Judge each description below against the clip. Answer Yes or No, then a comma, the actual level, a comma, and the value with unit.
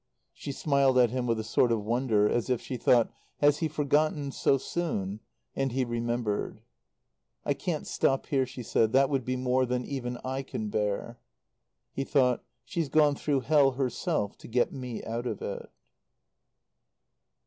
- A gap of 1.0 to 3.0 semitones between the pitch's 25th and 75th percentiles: Yes, average, 2.7 semitones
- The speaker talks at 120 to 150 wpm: No, average, 170 wpm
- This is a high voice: No, low, 130 Hz